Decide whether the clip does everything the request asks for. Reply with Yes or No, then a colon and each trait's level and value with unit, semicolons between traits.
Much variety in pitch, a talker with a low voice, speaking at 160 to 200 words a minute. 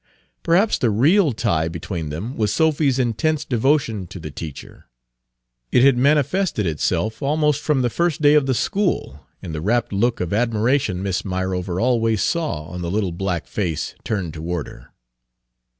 Yes: wide, 7.7 semitones; low, 110 Hz; average, 165 wpm